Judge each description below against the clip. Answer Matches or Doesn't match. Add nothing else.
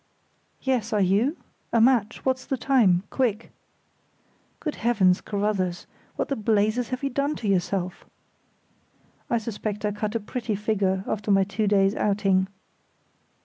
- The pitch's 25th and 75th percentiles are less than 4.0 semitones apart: Matches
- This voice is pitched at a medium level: Doesn't match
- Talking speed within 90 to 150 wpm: Matches